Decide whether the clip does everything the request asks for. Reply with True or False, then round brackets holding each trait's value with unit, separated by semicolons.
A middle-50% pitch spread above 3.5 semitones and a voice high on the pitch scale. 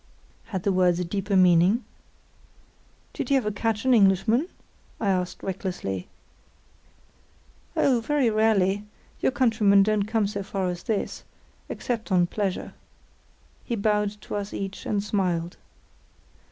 False (2.9 semitones; 200 Hz)